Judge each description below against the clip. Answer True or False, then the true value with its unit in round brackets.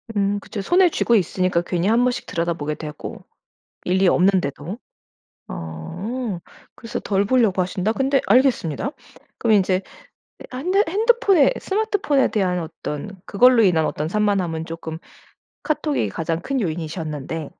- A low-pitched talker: False (195 Hz)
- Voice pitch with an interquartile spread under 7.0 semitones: False (7.3 semitones)